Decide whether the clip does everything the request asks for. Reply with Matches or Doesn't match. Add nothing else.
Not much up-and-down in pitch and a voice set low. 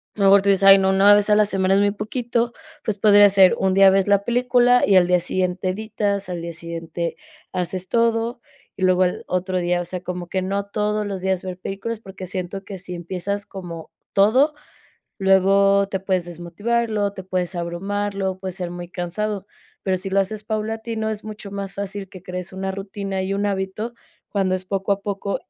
Doesn't match